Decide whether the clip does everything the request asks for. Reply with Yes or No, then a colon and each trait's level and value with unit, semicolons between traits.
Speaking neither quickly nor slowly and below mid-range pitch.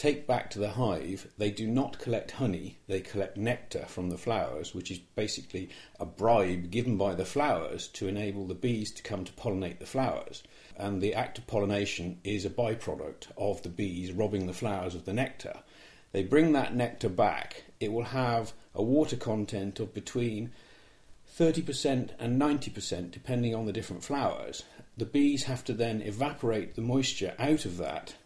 Yes: average, 180 wpm; low, 110 Hz